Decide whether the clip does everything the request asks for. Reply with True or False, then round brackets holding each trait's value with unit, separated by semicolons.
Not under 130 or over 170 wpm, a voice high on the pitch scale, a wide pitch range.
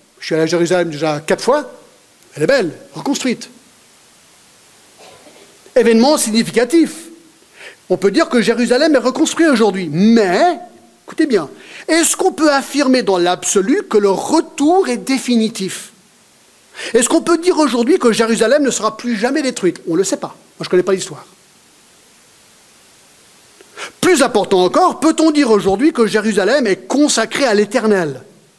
True (150 wpm; 240 Hz; 8.0 semitones)